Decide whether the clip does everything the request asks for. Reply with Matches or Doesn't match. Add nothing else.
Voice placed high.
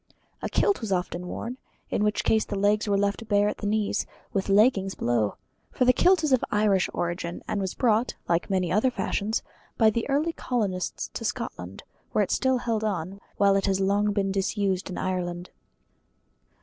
Matches